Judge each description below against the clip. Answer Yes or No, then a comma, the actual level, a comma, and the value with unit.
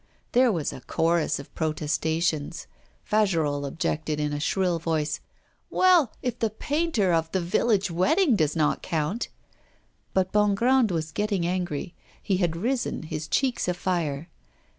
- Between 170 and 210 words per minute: No, average, 140 wpm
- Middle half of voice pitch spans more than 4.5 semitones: Yes, average, 5.2 semitones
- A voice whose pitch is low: No, medium, 175 Hz